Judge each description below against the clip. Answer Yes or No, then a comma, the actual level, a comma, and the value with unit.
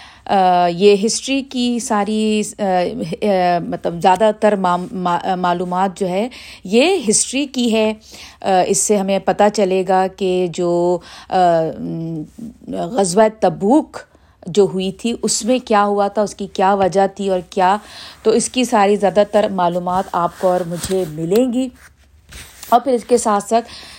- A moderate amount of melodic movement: Yes, average, 3.1 semitones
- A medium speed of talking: Yes, average, 145 wpm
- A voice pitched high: Yes, high, 200 Hz